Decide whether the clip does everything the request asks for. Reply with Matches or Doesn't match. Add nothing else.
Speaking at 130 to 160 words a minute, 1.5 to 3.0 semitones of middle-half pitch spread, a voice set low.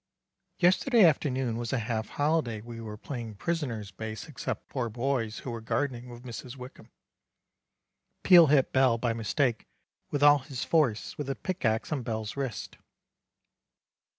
Doesn't match